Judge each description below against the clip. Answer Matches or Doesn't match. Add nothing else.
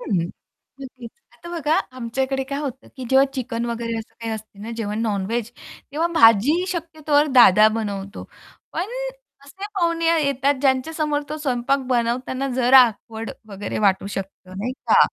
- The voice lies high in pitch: Matches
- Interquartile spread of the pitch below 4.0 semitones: Doesn't match